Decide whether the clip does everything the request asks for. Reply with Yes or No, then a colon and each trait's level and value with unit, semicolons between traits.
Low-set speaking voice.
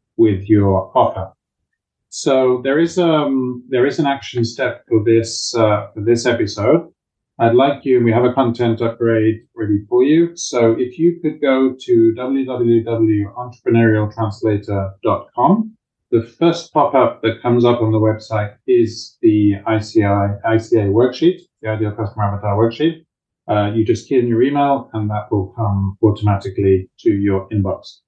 Yes: low, 115 Hz